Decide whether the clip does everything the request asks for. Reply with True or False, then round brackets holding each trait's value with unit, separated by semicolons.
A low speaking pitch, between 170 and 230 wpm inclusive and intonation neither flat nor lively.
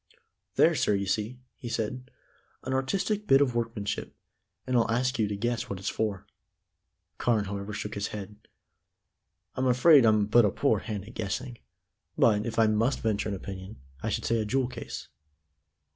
True (110 Hz; 175 wpm; 3.3 semitones)